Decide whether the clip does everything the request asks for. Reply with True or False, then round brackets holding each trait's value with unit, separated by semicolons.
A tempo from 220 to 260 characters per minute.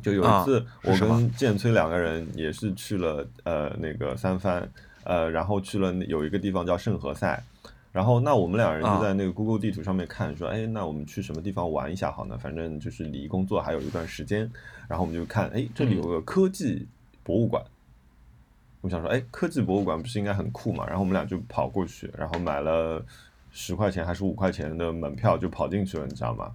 False (335 characters per minute)